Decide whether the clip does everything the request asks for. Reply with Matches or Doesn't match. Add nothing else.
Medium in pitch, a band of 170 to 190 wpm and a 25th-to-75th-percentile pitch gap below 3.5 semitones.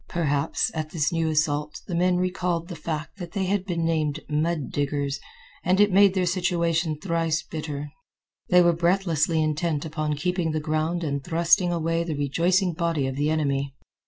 Matches